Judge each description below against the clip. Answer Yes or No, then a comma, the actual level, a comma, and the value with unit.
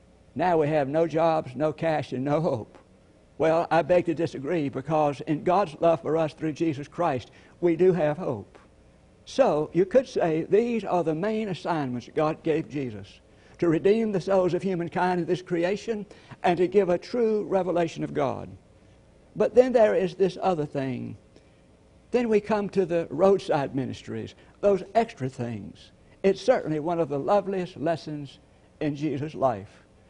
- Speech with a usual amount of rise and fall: Yes, average, 4.1 semitones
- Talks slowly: No, average, 165 wpm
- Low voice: No, medium, 165 Hz